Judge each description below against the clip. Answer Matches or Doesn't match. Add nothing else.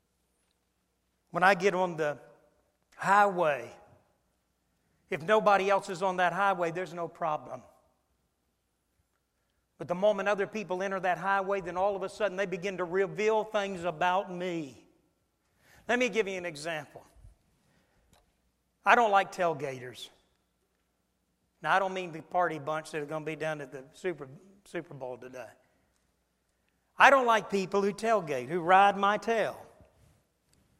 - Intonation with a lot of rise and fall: Matches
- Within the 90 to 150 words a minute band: Matches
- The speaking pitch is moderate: Matches